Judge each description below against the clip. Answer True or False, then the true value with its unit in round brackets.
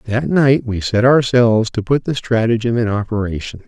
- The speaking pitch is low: True (115 Hz)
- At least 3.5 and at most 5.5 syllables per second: True (5.1 syllables/s)